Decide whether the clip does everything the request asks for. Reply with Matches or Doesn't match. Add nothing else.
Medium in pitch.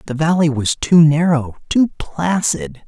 Matches